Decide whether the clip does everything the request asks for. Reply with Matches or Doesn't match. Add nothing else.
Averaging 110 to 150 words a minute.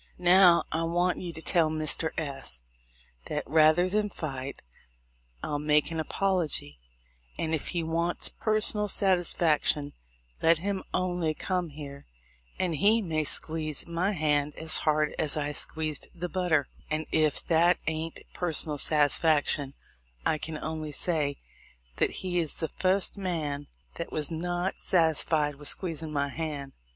Matches